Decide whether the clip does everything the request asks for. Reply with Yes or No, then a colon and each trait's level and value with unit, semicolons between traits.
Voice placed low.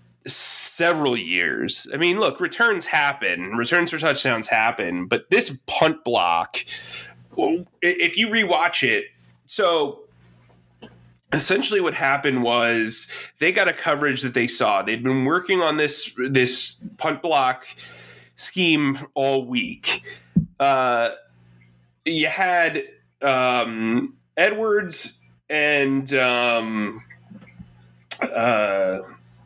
Yes: low, 125 Hz